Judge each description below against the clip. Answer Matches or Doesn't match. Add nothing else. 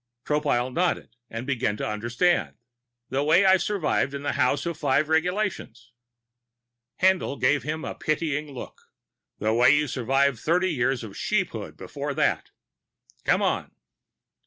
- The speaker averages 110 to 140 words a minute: Matches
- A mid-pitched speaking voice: Matches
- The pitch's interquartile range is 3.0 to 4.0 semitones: Doesn't match